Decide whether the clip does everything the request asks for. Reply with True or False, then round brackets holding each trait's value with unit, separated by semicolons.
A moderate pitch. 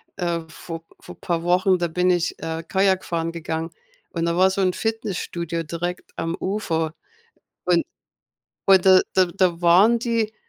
True (175 Hz)